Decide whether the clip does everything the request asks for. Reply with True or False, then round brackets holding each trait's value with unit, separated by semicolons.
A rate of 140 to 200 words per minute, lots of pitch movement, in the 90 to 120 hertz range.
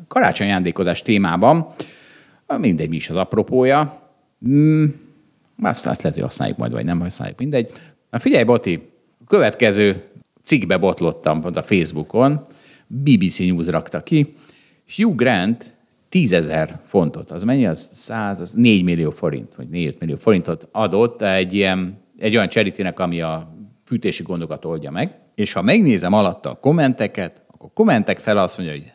True (155 wpm; 8.7 semitones; 100 Hz)